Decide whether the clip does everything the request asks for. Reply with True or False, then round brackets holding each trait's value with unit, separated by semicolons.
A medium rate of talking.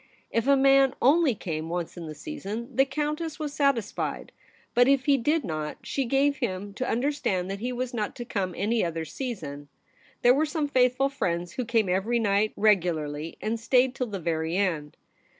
True (190 wpm)